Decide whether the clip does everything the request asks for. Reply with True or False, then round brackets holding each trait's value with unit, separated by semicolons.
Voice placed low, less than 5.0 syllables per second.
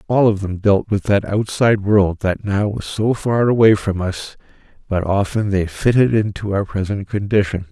True (100 Hz; 4.7 syllables/s)